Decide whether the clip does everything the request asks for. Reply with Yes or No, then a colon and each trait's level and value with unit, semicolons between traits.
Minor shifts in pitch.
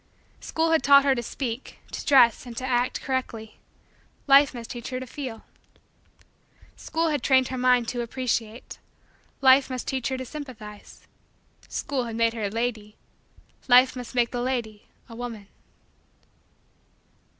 Yes: narrow, 2.3 semitones